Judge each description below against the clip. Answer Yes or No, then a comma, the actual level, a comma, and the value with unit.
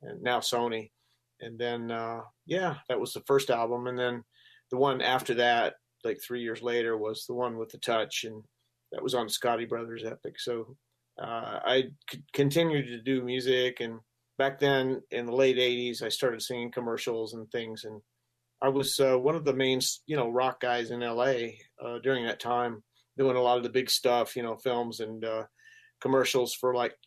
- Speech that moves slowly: No, average, 195 wpm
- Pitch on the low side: Yes, low, 120 Hz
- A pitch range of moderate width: No, narrow, 1.9 semitones